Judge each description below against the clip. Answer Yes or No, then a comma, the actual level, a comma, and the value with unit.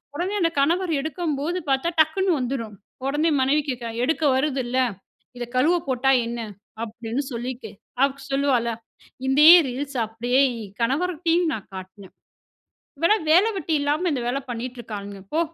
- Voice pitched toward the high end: Yes, very high, 270 Hz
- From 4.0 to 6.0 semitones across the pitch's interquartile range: Yes, average, 5.0 semitones